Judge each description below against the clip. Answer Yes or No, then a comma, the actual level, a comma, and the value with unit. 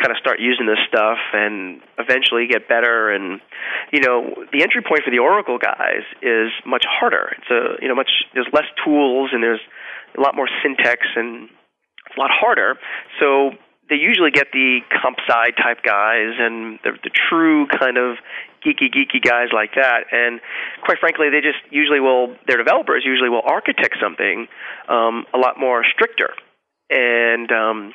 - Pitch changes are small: No, average, 3.9 semitones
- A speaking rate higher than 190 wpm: No, average, 175 wpm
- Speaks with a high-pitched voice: No, low, 125 Hz